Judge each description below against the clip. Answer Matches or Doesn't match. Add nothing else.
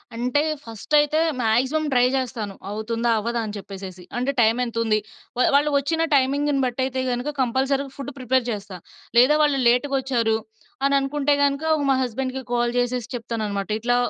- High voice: Matches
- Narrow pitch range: Doesn't match